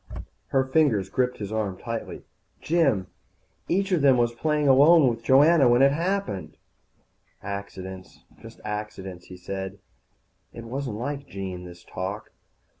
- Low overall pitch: Yes, low, 115 Hz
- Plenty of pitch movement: Yes, wide, 6.4 semitones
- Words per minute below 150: Yes, slow, 135 wpm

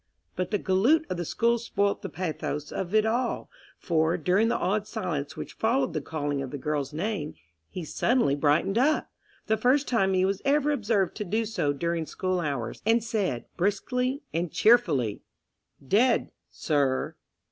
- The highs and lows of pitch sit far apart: Yes, wide, 6.5 semitones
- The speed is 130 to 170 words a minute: Yes, average, 160 wpm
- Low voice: No, high, 190 Hz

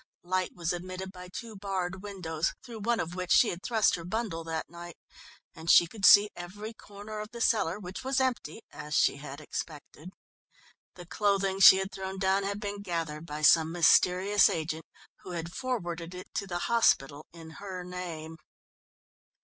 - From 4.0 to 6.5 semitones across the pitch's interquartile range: No, average, 3.3 semitones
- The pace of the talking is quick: No, average, 175 wpm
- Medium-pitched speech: Yes, medium, 180 Hz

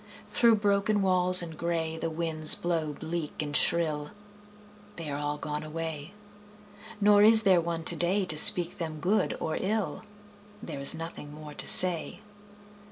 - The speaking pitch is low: No, medium, 165 Hz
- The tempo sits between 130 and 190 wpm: Yes, average, 155 wpm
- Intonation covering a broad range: No, average, 3.1 semitones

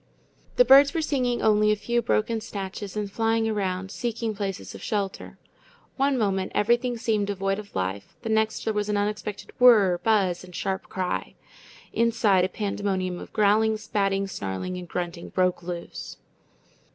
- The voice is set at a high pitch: Yes, high, 205 Hz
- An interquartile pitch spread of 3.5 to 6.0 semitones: No, average, 2.8 semitones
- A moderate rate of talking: Yes, average, 160 wpm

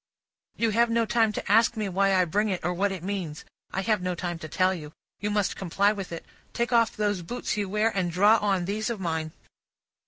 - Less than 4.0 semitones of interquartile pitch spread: Yes, average, 3.1 semitones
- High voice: Yes, high, 200 Hz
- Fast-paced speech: Yes, fast, 230 wpm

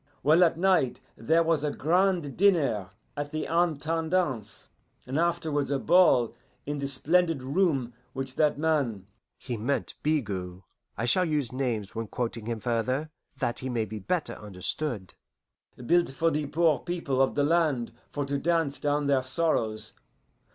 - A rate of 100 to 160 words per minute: Yes, average, 155 wpm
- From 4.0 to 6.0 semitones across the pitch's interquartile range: Yes, average, 5.2 semitones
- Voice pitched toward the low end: No, medium, 145 Hz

